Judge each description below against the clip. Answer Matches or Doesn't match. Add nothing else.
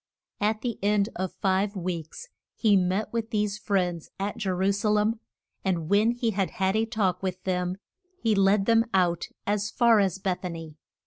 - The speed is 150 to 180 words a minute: Doesn't match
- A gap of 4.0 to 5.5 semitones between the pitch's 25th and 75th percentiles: Doesn't match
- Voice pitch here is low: Doesn't match